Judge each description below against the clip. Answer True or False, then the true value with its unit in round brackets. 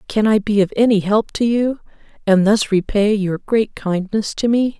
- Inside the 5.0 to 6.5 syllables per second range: False (4.6 syllables/s)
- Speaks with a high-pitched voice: True (210 Hz)